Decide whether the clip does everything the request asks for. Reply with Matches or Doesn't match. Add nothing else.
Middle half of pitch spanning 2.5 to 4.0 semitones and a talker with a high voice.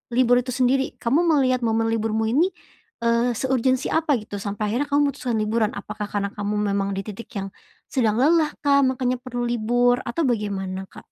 Matches